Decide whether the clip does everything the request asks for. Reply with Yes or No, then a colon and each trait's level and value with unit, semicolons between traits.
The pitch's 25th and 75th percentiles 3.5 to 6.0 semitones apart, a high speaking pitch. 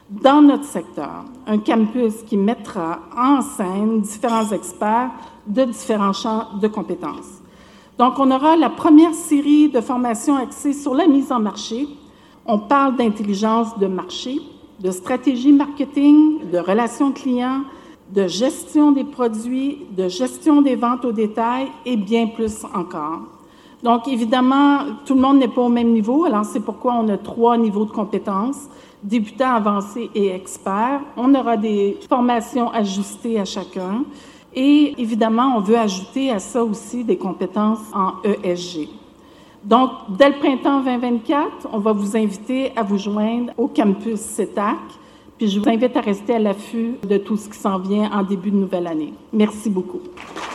Yes: average, 4.5 semitones; high, 235 Hz